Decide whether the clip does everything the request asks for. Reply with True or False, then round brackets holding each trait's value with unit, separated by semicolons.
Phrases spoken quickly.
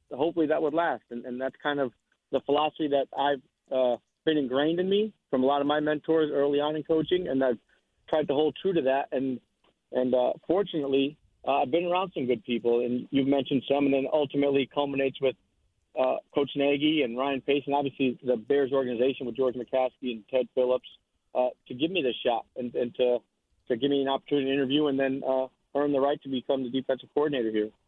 True (215 wpm)